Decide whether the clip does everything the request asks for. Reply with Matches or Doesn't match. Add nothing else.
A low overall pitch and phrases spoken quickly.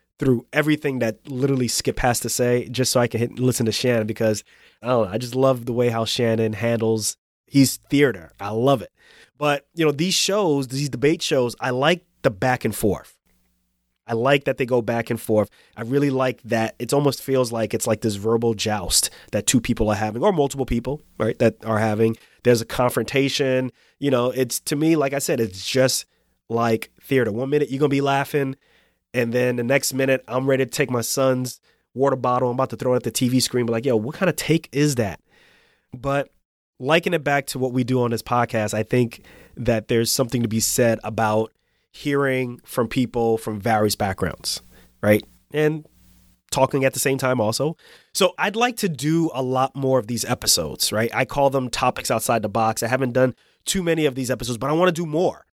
Matches